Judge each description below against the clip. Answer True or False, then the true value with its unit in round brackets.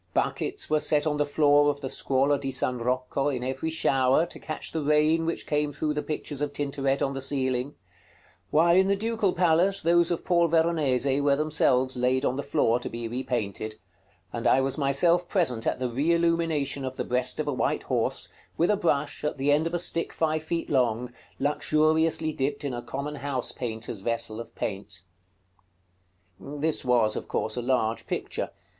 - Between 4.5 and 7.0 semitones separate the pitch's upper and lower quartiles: False (3.7 semitones)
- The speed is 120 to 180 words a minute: False (190 wpm)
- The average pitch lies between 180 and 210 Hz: False (145 Hz)